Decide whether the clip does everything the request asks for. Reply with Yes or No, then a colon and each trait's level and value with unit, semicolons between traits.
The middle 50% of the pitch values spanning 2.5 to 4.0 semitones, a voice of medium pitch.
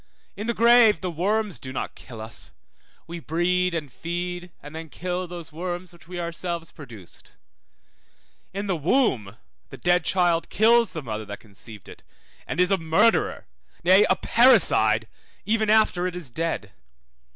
Yes: average, 3.5 semitones; medium, 175 Hz